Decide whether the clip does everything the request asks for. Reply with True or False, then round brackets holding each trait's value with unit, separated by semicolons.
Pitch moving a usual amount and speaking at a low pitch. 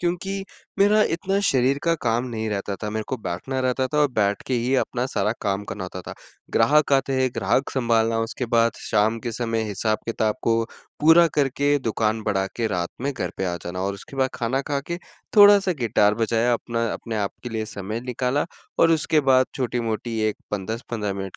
True (3.9 semitones; 115 Hz)